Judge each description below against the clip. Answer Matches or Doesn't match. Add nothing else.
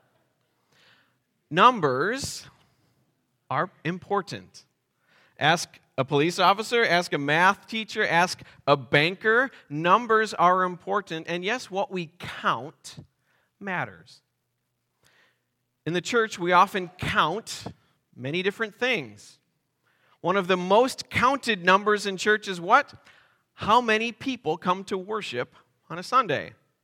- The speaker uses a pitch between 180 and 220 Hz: Matches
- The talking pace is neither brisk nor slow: Doesn't match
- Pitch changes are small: Doesn't match